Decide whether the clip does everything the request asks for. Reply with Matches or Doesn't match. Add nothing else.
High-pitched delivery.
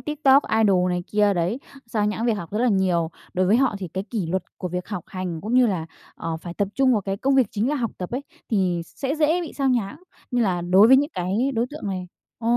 Matches